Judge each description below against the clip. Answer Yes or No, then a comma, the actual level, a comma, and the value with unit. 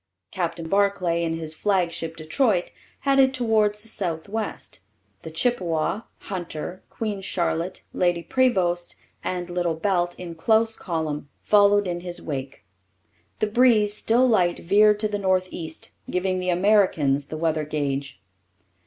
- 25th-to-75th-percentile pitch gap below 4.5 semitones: Yes, average, 4.1 semitones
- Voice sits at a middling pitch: Yes, medium, 180 Hz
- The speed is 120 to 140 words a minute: Yes, slow, 135 wpm